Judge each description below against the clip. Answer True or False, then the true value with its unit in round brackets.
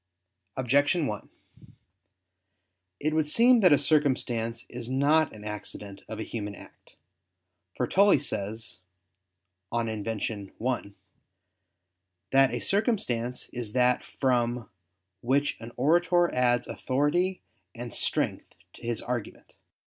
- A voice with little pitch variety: False (4.4 semitones)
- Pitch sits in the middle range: False (125 Hz)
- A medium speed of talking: False (115 wpm)